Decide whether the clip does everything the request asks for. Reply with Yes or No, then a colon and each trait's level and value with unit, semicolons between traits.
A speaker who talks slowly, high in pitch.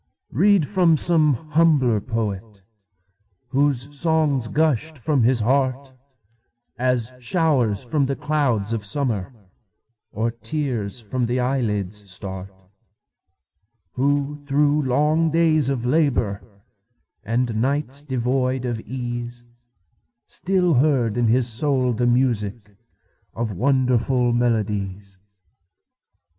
No: slow, 85 wpm; low, 120 Hz